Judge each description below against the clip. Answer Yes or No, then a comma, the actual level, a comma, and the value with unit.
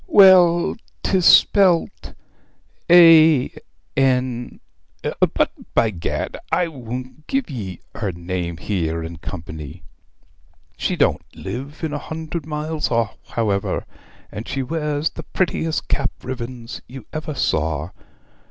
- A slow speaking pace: Yes, slow, 115 wpm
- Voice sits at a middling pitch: No, low, 130 Hz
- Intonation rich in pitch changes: Yes, wide, 8.2 semitones